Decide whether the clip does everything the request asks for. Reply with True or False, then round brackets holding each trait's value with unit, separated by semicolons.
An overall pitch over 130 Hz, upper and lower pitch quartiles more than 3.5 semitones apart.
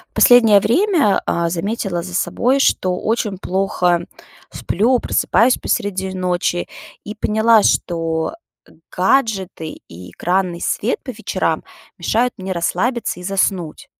True (190 Hz; 4.2 semitones)